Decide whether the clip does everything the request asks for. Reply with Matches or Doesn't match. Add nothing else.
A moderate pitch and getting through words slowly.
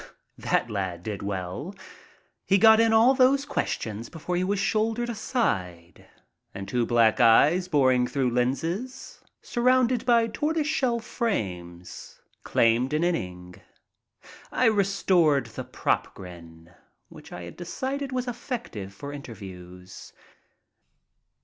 Matches